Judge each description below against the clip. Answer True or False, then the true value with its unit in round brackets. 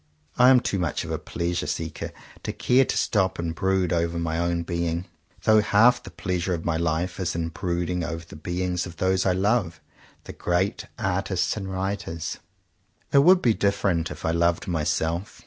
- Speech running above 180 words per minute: True (190 wpm)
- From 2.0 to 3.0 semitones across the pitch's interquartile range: True (2.5 semitones)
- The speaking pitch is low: True (90 Hz)